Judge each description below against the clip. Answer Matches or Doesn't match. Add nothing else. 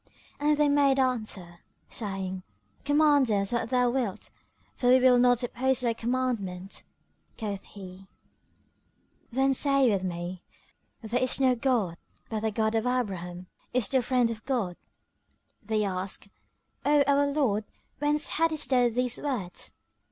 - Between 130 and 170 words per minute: Matches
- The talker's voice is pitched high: Matches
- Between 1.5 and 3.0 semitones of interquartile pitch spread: Doesn't match